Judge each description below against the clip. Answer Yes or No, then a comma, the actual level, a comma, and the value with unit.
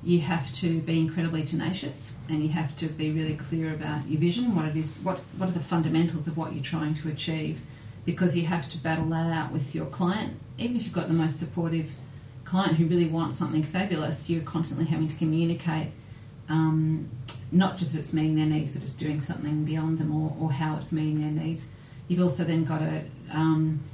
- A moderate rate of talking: No, fast, 215 wpm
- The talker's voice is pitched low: No, medium, 155 Hz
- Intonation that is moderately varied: No, narrow, 1.5 semitones